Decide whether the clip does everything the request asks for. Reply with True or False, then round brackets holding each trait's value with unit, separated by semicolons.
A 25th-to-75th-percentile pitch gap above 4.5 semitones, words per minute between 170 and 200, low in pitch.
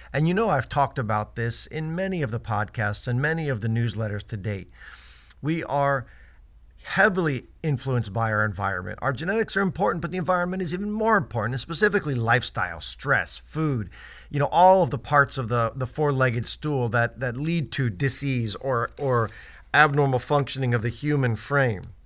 True (5.2 semitones; 180 wpm; 130 Hz)